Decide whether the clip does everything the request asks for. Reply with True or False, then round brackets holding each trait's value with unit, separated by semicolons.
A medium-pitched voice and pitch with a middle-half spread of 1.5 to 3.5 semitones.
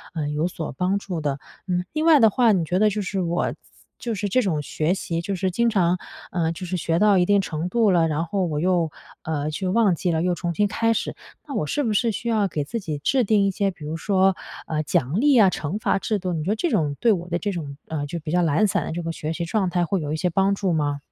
False (180 Hz; 4.0 semitones)